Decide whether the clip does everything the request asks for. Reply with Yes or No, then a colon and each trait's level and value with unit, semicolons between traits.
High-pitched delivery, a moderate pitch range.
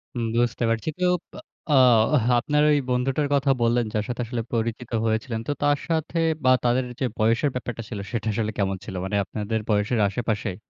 No: low, 120 Hz; average, 3.0 semitones